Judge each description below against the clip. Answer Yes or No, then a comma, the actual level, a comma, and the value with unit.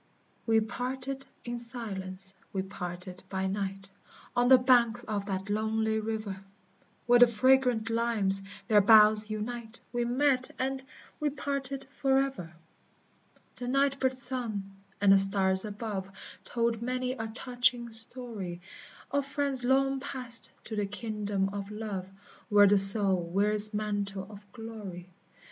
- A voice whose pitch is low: No, high, 220 Hz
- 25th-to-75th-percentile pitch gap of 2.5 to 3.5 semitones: No, average, 4.0 semitones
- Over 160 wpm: No, slow, 135 wpm